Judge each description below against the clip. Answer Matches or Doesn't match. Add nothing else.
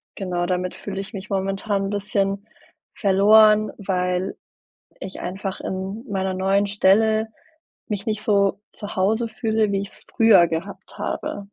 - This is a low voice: Doesn't match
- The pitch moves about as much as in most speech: Doesn't match